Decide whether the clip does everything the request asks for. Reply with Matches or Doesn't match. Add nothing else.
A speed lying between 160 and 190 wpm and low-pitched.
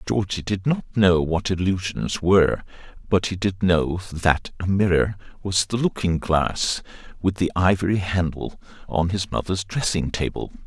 Doesn't match